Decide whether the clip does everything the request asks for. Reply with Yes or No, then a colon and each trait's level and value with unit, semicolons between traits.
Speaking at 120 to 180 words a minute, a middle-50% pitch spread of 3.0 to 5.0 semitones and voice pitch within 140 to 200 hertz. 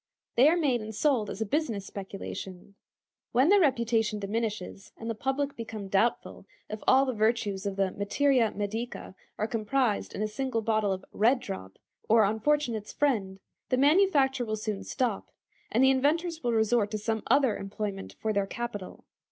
No: average, 170 wpm; average, 4.3 semitones; high, 225 Hz